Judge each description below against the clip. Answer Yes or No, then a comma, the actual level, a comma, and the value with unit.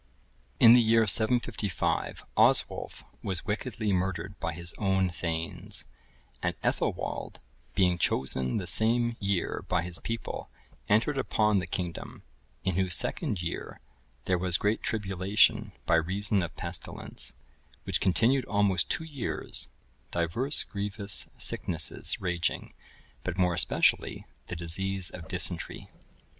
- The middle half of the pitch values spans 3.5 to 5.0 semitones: Yes, average, 3.8 semitones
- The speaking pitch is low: Yes, very low, 95 Hz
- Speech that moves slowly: Yes, slow, 125 wpm